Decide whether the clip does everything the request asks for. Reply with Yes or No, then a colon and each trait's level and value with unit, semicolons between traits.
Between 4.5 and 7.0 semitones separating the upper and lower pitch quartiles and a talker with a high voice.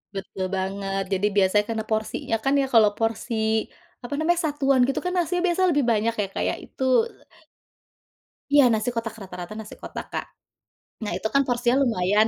Yes: average, 4.9 semitones; high, 225 Hz